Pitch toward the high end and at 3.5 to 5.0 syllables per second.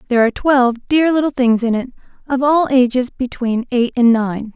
No: very high, 250 Hz; 5.4 syllables/s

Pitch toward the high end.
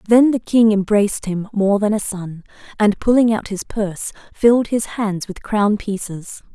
Yes: high, 210 Hz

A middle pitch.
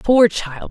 No: high, 200 Hz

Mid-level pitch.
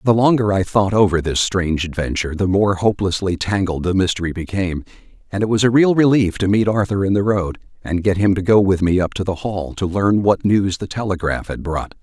No: very low, 95 Hz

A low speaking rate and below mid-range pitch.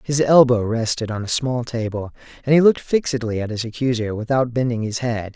No: average, 200 wpm; low, 120 Hz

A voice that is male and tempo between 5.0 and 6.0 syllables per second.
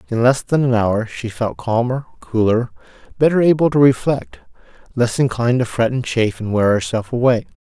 Yes: male; 5.4 syllables/s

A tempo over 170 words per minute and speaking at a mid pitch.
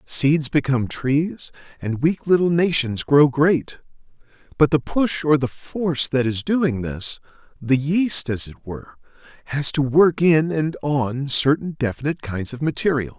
No: average, 160 wpm; medium, 145 Hz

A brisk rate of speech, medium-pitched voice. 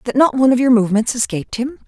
No: fast, 255 wpm; high, 245 Hz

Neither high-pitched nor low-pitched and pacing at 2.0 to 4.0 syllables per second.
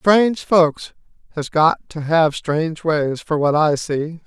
Yes: medium, 160 Hz; 3.8 syllables/s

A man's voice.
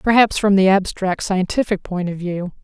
No: female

